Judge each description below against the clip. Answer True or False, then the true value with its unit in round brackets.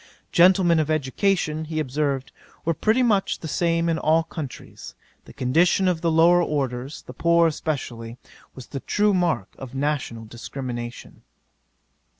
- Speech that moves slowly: False (145 wpm)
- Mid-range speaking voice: True (155 Hz)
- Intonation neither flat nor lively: True (4.3 semitones)